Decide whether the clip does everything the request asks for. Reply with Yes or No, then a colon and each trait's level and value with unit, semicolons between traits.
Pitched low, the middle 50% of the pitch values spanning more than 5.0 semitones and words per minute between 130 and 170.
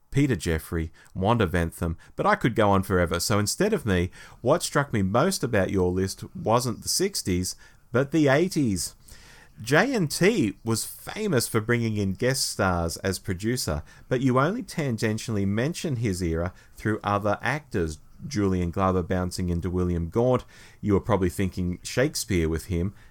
Yes: low, 105 Hz; wide, 5.6 semitones; average, 160 wpm